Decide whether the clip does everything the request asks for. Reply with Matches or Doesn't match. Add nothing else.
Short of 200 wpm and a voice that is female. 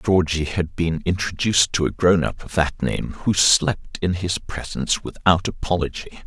Doesn't match